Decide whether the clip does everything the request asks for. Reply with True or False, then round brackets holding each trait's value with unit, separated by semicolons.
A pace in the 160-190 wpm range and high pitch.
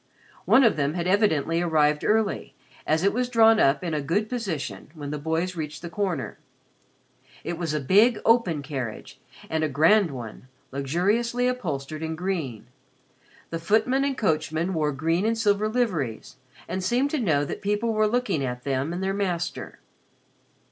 False (170 wpm; 175 Hz)